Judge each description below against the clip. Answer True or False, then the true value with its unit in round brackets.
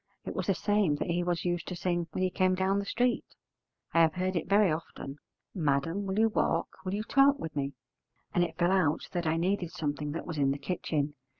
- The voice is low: False (175 Hz)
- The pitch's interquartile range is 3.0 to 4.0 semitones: True (3.3 semitones)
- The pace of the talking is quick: True (230 wpm)